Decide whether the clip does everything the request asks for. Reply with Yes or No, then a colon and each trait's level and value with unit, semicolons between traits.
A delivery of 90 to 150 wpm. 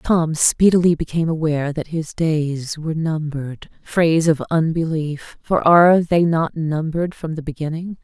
Yes: average, 140 wpm